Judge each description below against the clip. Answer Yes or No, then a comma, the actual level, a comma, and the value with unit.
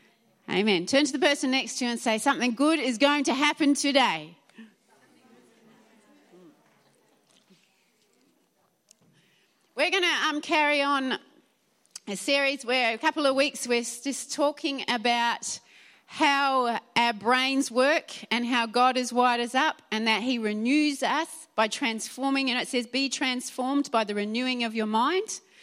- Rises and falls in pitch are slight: No, average, 3.6 semitones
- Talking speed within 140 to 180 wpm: Yes, average, 150 wpm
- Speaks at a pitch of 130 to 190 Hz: No, very high, 255 Hz